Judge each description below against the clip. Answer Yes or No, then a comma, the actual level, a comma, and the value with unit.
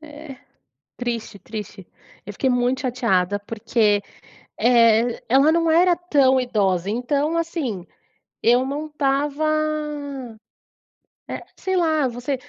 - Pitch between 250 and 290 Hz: Yes, very high, 255 Hz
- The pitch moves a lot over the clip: No, average, 4.8 semitones